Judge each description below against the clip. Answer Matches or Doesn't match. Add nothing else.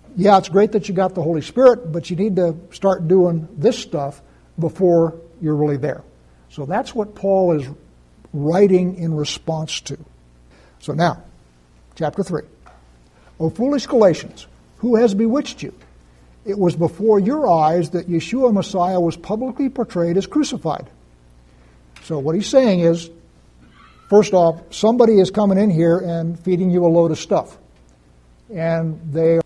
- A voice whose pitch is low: Doesn't match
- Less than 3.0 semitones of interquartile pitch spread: Doesn't match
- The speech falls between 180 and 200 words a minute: Doesn't match